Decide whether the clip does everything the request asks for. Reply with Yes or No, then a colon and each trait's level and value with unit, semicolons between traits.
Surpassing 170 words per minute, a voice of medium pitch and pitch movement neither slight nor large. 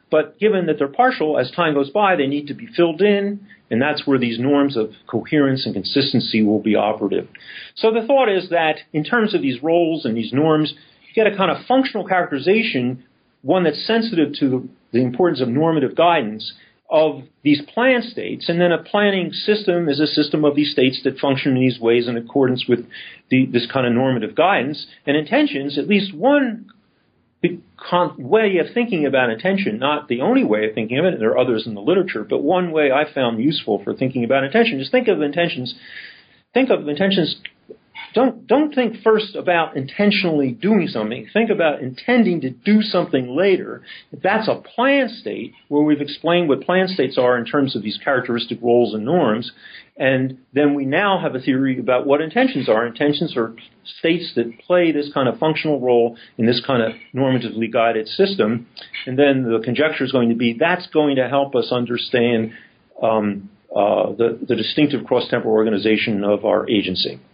No: average, 190 wpm; medium, 145 Hz; wide, 6.7 semitones